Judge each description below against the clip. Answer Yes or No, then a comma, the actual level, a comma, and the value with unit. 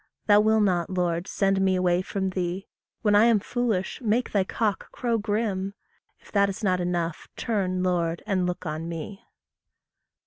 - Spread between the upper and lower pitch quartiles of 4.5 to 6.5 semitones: No, average, 2.7 semitones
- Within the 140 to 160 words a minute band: No, average, 170 wpm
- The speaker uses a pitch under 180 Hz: No, high, 190 Hz